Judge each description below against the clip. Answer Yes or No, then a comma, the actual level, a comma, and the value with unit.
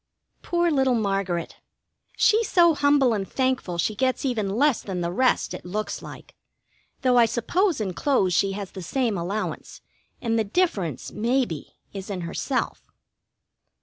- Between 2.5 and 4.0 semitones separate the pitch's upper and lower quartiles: No, wide, 5.6 semitones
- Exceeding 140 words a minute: Yes, average, 150 wpm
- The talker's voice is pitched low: No, high, 225 Hz